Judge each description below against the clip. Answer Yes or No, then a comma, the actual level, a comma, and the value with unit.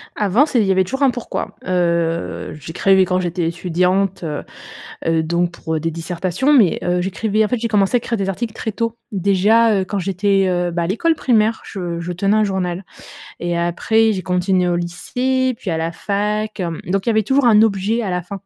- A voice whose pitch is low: No, high, 190 Hz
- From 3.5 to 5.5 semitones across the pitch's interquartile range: Yes, average, 3.8 semitones